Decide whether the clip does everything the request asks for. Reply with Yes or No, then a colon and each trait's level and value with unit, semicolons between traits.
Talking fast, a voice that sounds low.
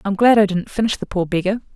No: fast, 275 wpm; high, 200 Hz